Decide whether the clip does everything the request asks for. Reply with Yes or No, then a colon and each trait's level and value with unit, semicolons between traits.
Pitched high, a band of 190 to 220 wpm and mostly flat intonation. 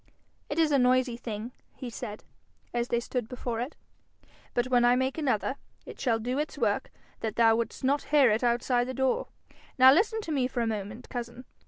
Yes: high, 245 Hz; average, 200 wpm; narrow, 2.0 semitones